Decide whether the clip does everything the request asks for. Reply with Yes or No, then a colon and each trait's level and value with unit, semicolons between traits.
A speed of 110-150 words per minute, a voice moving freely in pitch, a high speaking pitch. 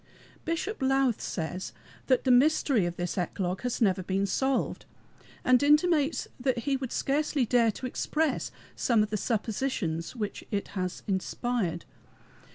Yes: average, 145 wpm; wide, 5.9 semitones; high, 245 Hz